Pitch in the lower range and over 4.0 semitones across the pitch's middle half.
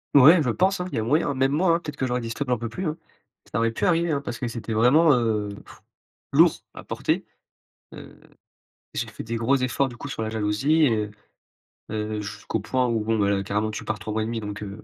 Yes: low, 115 Hz; average, 4.5 semitones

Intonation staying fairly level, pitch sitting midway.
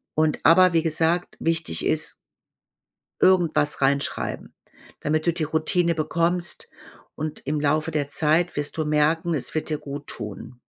Yes: narrow, 2.1 semitones; medium, 155 Hz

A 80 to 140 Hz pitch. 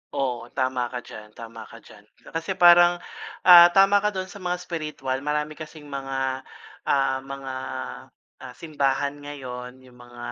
Yes: low, 135 Hz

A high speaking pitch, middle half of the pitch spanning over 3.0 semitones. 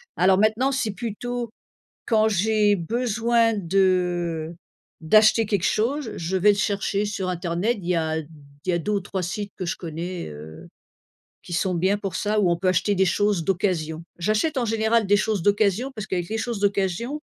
Yes: high, 200 Hz; average, 3.6 semitones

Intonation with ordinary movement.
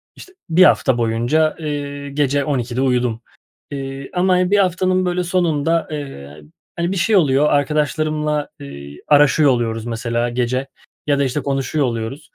Yes: average, 4.4 semitones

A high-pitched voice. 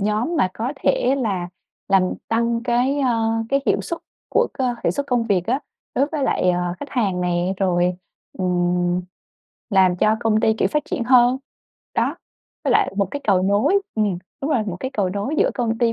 Yes: high, 220 Hz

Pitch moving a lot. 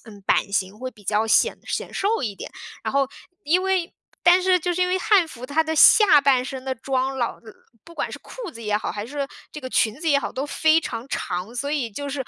Yes: wide, 6.2 semitones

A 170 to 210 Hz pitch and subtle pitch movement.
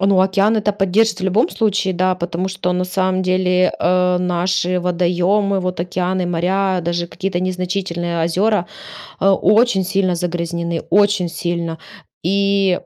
Yes: medium, 185 Hz; narrow, 1.8 semitones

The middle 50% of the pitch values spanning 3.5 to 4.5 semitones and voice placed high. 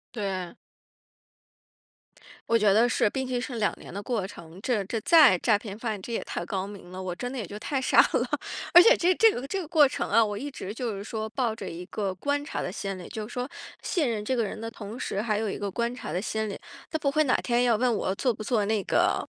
Yes: average, 3.8 semitones; high, 220 Hz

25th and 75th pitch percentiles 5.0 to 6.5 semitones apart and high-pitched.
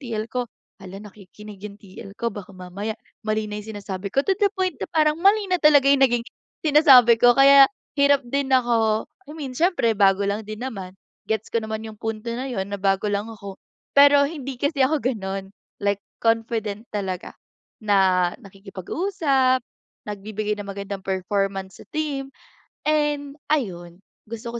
Yes: wide, 5.6 semitones; high, 220 Hz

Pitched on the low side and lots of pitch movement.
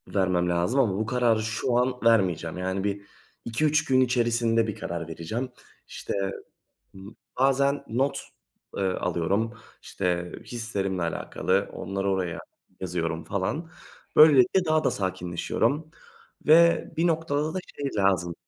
Yes: low, 110 Hz; wide, 6.4 semitones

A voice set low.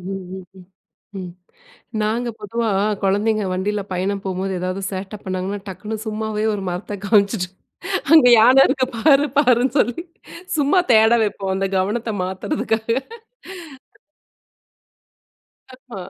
No: high, 210 Hz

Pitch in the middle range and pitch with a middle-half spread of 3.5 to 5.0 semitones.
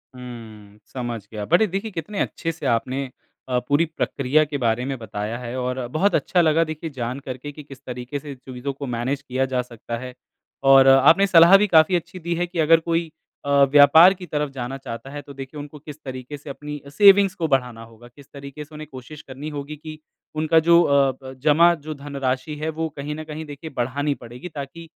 Yes: medium, 145 Hz; average, 3.8 semitones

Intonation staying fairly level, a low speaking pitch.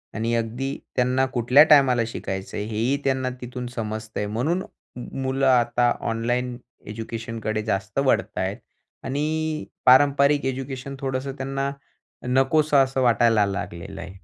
No: average, 3.2 semitones; low, 125 Hz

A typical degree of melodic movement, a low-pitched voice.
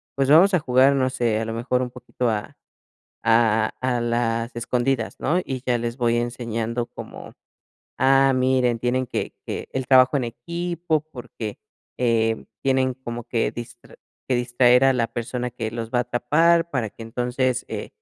No: narrow, 2.0 semitones; low, 125 Hz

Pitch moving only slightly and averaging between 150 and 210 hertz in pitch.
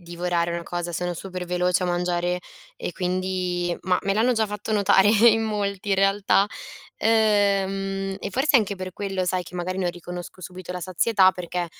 Yes: narrow, 2.1 semitones; medium, 185 Hz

